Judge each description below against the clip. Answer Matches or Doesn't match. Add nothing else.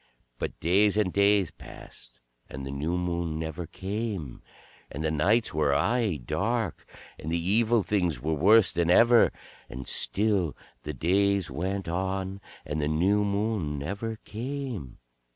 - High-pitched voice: Doesn't match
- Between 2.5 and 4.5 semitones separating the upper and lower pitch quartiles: Doesn't match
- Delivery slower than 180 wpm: Matches